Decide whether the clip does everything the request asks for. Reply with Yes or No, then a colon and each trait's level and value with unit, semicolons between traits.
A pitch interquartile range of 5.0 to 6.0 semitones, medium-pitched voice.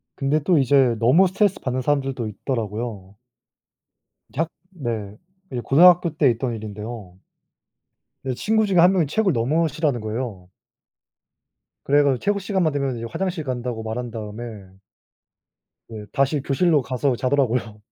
No: wide, 5.4 semitones; low, 130 Hz